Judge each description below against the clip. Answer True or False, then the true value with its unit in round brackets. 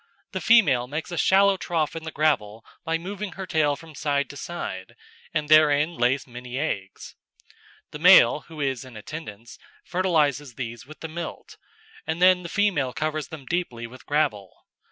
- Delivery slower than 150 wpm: False (170 wpm)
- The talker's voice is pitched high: False (150 Hz)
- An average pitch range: True (4.8 semitones)